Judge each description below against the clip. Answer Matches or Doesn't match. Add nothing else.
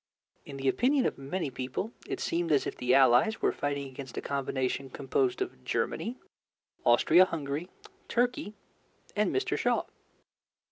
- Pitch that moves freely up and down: Matches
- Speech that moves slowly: Doesn't match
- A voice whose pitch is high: Doesn't match